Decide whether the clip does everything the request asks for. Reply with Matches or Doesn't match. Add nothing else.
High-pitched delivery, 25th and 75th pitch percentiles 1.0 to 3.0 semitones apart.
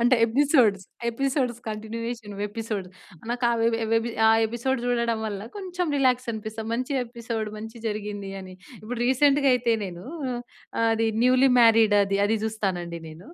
Matches